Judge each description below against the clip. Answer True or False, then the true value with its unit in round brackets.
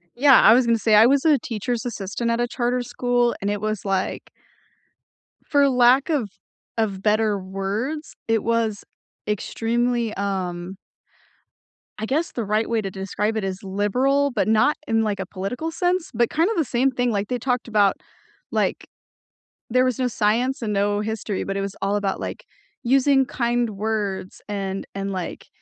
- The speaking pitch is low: False (225 Hz)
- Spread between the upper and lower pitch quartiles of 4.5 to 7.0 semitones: False (3.7 semitones)